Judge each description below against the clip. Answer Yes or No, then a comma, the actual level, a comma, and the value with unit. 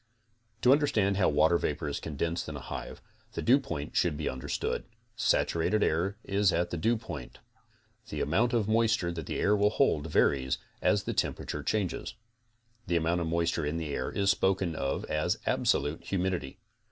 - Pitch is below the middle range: Yes, very low, 85 Hz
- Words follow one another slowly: No, average, 175 wpm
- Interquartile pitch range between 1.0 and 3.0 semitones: No, average, 5.0 semitones